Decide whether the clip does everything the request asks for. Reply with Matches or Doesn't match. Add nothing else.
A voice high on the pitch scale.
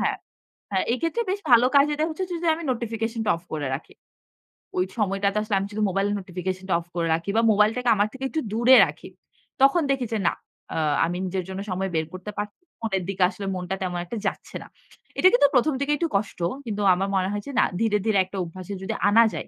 Matches